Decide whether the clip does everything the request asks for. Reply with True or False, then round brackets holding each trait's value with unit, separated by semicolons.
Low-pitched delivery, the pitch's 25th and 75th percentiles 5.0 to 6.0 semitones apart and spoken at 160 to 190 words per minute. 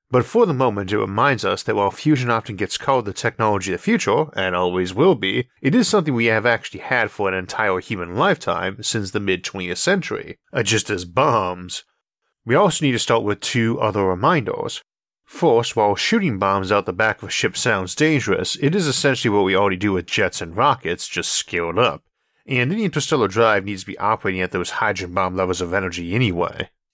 False (105 Hz; 5.5 semitones; 205 wpm)